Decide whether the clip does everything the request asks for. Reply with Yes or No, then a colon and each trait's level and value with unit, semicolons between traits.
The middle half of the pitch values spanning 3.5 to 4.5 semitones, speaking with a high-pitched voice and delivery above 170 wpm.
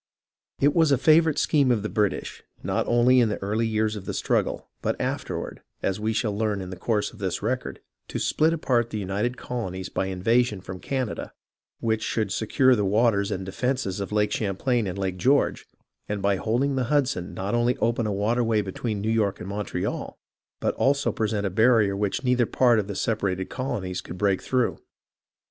No: average, 3.8 semitones; low, 110 Hz; average, 200 wpm